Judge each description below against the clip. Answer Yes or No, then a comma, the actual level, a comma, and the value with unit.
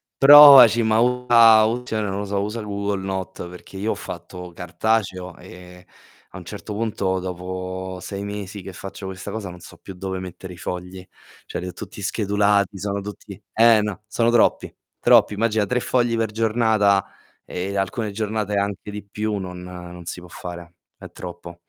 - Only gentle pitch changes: No, average, 3.0 semitones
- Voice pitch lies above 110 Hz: No, low, 100 Hz